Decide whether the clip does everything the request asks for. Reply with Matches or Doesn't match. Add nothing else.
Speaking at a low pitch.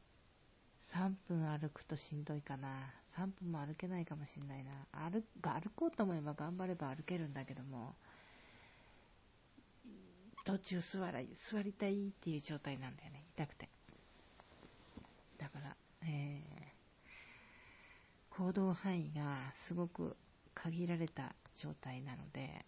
Doesn't match